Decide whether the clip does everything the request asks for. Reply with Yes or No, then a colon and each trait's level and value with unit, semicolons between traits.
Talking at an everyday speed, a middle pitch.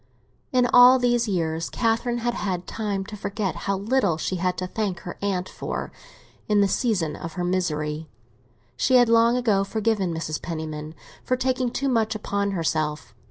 No: average, 170 wpm; high, 200 Hz